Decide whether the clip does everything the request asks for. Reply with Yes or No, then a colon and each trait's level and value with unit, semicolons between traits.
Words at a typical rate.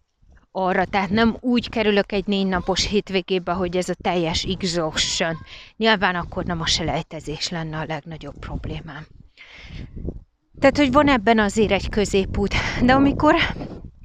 Yes: average, 135 wpm